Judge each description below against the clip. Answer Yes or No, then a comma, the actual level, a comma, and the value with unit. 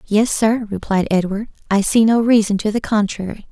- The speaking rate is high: No, average, 190 wpm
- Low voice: No, high, 210 Hz